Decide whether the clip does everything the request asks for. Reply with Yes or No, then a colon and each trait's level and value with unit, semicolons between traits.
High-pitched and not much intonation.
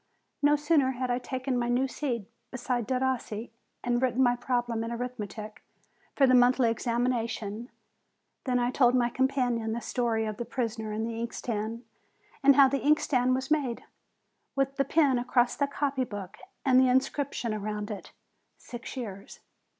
Yes: high, 245 Hz; narrow, 2.2 semitones